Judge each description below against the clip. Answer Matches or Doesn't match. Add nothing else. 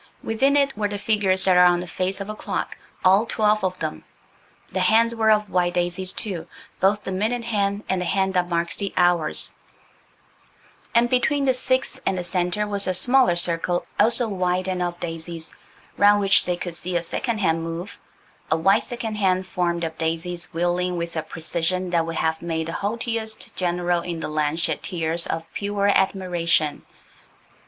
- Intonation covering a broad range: Doesn't match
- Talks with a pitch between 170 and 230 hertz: Matches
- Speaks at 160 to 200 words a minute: Matches